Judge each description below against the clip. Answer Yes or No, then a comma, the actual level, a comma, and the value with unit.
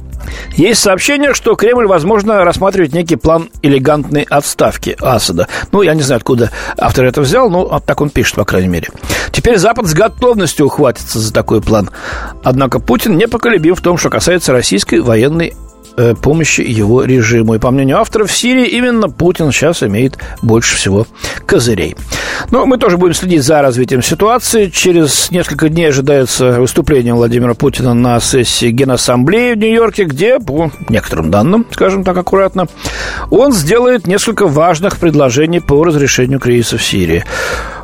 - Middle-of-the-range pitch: Yes, medium, 145 Hz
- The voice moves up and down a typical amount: No, wide, 7.0 semitones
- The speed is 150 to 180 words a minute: Yes, average, 155 wpm